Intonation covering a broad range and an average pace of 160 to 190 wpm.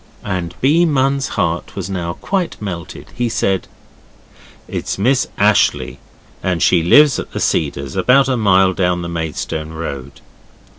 No: wide, 7.2 semitones; average, 145 wpm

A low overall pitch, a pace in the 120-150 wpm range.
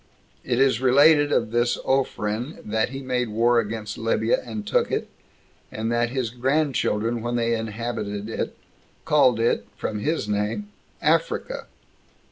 Yes: low, 120 Hz; average, 140 wpm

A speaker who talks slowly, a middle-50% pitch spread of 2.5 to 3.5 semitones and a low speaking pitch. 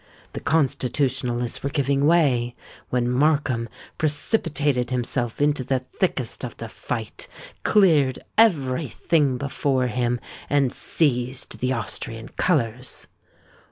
Yes: slow, 110 wpm; average, 2.9 semitones; low, 130 Hz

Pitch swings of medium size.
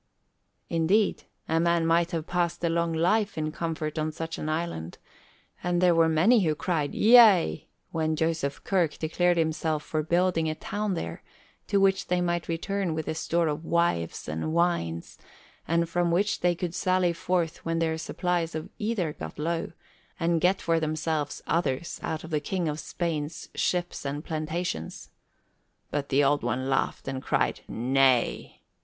No: narrow, 2.2 semitones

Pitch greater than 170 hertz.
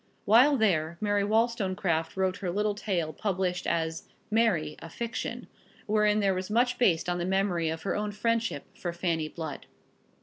Yes: high, 190 Hz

